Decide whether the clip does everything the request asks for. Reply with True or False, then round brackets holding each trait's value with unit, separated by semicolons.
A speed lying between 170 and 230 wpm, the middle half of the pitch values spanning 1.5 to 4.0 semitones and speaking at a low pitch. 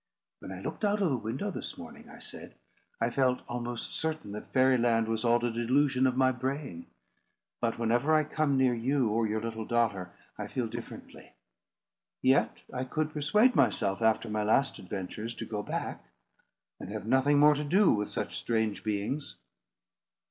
False (175 wpm; 4.4 semitones; 125 Hz)